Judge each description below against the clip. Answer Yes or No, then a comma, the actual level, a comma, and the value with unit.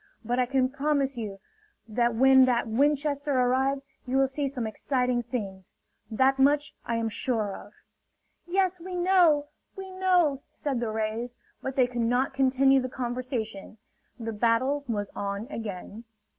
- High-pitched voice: Yes, very high, 255 Hz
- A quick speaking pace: No, average, 155 wpm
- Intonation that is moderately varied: Yes, average, 3.5 semitones